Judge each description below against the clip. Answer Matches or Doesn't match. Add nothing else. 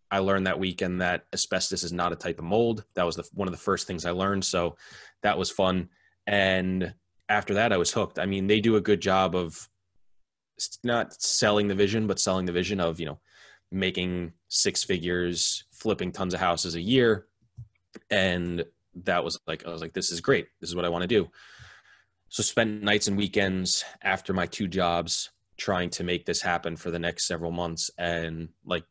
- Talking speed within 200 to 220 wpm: Matches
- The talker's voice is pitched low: Matches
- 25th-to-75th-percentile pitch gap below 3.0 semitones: Matches